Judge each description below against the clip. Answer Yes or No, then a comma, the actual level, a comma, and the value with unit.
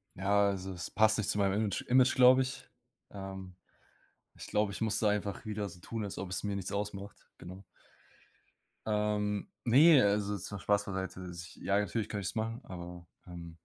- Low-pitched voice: Yes, low, 100 Hz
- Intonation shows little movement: Yes, narrow, 2.0 semitones